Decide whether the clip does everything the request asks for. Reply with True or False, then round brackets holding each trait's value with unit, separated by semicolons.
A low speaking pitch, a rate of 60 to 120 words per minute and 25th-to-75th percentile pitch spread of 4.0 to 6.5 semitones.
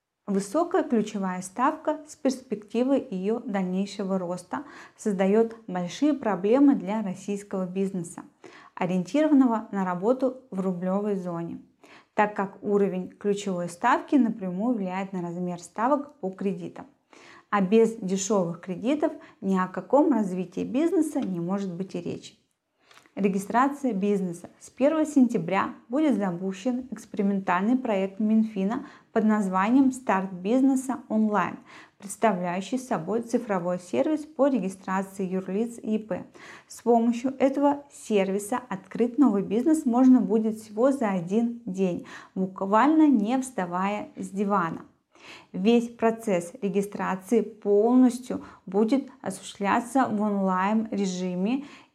False (215 Hz; 110 wpm; 4.9 semitones)